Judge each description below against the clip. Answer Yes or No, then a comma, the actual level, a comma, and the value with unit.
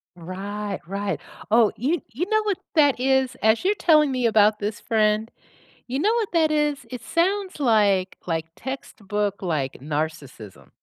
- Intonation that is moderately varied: No, wide, 7.1 semitones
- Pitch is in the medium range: No, high, 220 Hz